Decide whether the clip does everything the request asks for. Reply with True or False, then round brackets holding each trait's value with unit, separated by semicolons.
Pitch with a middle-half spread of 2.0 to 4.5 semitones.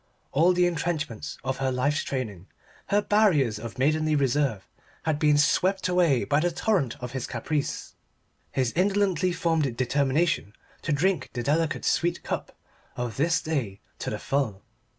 False (5.0 semitones)